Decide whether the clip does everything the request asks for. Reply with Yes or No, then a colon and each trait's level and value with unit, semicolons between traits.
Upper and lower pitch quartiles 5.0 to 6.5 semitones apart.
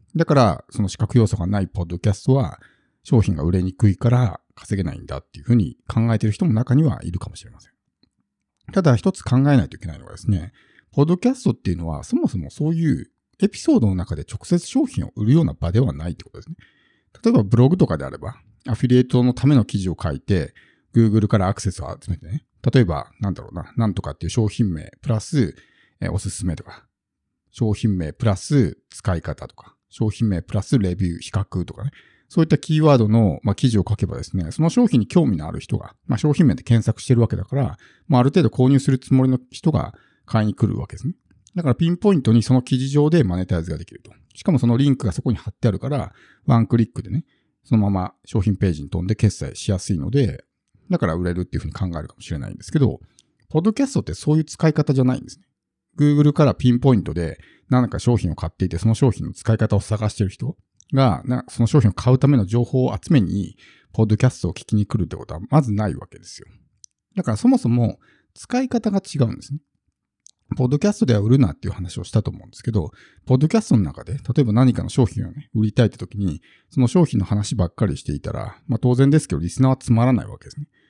Yes: wide, 5.4 semitones